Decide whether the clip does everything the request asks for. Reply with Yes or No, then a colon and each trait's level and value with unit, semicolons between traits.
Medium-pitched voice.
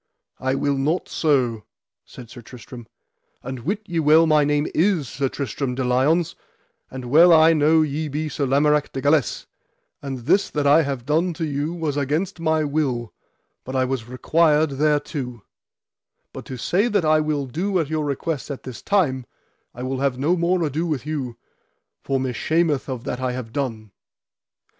Yes: medium, 145 Hz